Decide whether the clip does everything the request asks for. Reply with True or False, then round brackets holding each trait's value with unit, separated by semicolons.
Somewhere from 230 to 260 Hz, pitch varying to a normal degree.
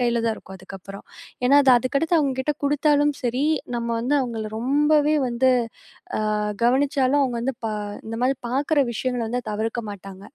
True (255 Hz; 3.7 semitones)